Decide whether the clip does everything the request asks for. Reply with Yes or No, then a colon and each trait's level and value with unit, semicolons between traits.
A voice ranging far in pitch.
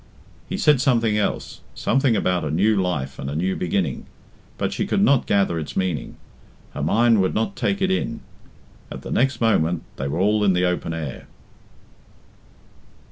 Yes: wide, 5.7 semitones